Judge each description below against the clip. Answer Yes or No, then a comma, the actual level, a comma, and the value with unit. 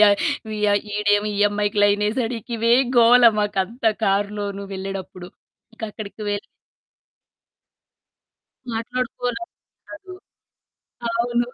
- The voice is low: No, high, 210 Hz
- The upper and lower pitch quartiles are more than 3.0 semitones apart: No, narrow, 2.4 semitones